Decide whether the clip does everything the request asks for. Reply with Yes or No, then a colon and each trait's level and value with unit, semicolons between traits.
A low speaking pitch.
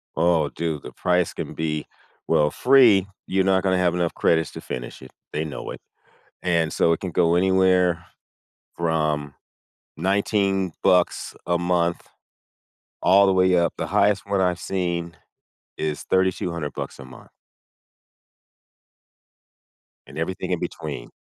Yes: very low, 85 Hz